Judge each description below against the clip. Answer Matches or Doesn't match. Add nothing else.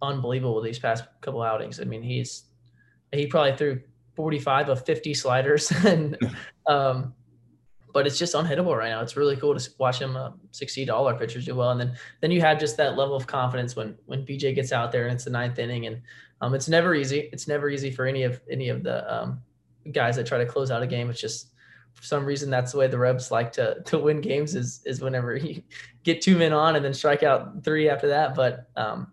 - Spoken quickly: Matches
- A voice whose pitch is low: Matches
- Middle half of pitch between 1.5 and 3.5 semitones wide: Matches